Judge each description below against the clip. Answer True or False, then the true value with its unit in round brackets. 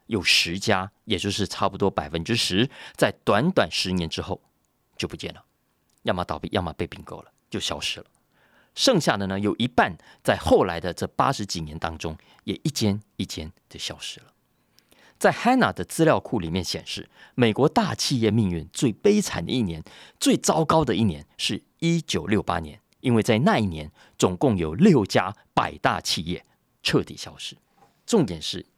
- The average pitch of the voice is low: True (100 Hz)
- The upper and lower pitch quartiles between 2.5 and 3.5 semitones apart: False (5.2 semitones)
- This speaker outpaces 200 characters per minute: True (265 characters per minute)